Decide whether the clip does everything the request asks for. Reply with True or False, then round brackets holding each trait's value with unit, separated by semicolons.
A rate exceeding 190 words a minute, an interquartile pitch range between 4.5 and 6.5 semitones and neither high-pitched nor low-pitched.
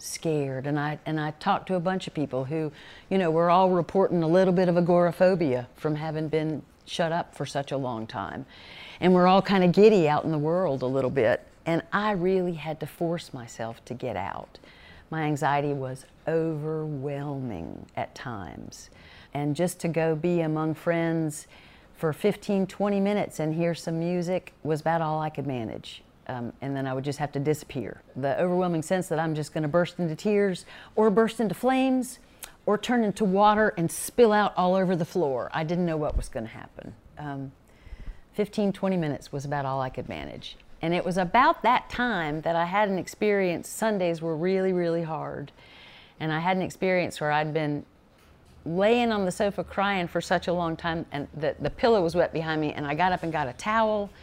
False (205 wpm; 3.9 semitones; 165 Hz)